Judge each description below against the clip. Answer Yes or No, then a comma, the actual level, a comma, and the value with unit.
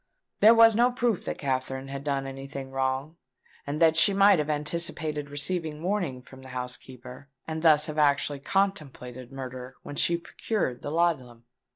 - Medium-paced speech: Yes, average, 170 wpm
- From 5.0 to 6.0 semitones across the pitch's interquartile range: No, average, 4.2 semitones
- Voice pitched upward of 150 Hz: No, medium, 145 Hz